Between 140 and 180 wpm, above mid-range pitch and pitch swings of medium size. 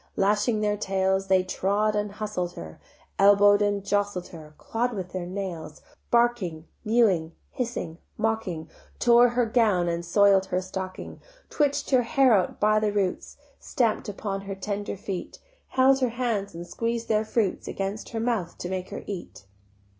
Yes: average, 160 wpm; high, 205 Hz; average, 3.2 semitones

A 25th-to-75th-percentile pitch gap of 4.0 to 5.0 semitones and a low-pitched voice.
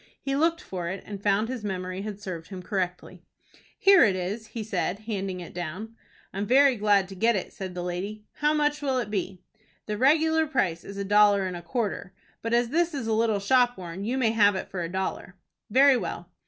No: average, 4.6 semitones; high, 205 Hz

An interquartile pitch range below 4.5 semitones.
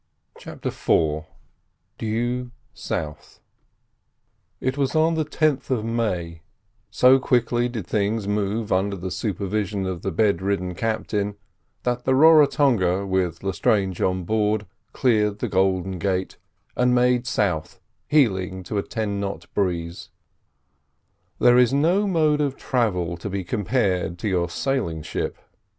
No: average, 4.9 semitones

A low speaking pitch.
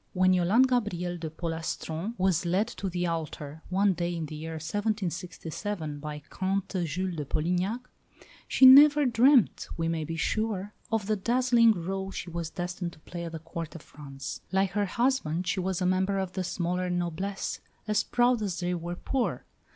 No: medium, 180 Hz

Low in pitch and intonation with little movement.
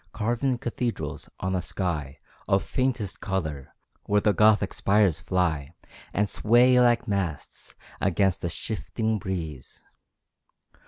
No: low, 100 Hz; average, 4.5 semitones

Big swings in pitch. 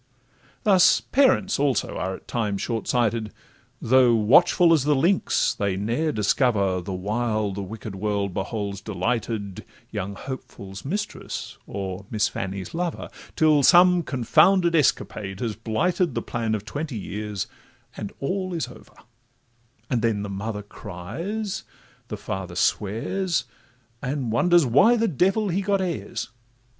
Yes: wide, 8.4 semitones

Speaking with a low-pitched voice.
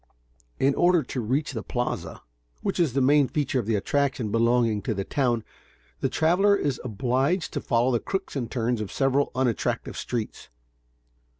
Yes: low, 130 Hz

